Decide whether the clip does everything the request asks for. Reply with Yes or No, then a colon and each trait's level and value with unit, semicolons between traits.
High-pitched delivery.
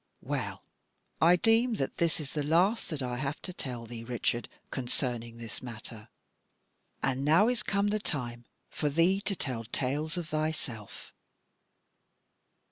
No: medium, 145 Hz